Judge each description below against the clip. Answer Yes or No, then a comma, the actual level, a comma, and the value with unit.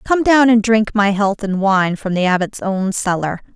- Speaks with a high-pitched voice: Yes, high, 205 Hz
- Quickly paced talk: Yes, fast, 220 wpm